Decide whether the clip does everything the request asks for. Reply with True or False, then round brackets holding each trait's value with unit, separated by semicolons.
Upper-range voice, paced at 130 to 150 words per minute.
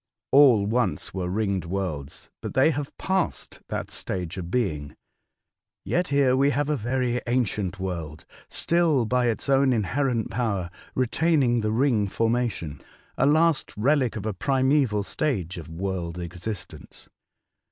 False (115 Hz; 140 wpm)